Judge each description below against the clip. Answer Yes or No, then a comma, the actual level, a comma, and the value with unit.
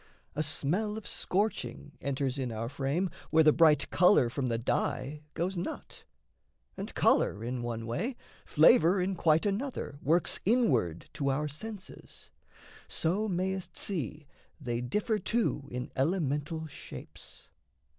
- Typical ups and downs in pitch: No, wide, 6.1 semitones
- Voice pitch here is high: No, medium, 155 Hz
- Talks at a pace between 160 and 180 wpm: No, slow, 135 wpm